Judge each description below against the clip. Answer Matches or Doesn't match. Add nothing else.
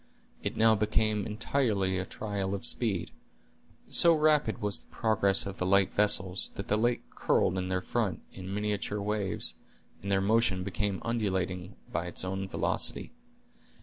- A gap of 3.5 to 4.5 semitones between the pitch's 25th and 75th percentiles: Doesn't match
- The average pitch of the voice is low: Matches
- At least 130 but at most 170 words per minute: Matches